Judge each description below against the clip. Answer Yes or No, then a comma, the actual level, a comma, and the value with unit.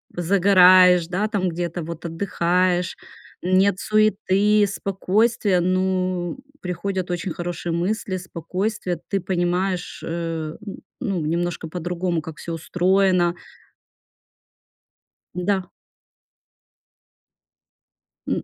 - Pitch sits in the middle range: Yes, medium, 180 Hz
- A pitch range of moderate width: No, narrow, 2.0 semitones